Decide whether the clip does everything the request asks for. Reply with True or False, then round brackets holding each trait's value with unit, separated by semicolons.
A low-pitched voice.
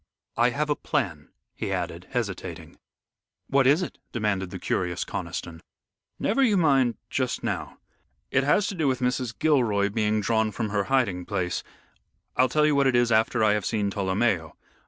True (115 Hz)